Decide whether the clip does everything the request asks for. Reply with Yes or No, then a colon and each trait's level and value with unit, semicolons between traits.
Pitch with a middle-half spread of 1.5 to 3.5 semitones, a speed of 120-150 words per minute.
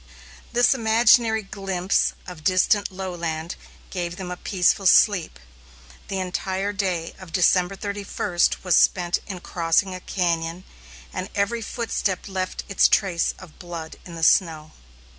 Yes: narrow, 2.4 semitones; slow, 135 wpm